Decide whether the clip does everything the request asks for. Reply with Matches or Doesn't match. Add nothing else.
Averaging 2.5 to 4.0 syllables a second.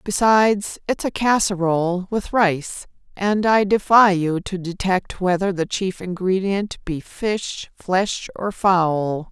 Matches